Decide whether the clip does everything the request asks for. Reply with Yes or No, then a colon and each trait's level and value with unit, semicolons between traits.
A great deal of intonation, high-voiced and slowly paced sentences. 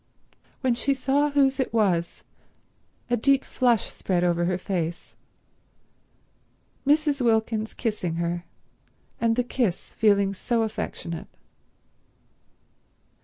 Yes: wide, 6.4 semitones; high, 225 Hz; slow, 105 wpm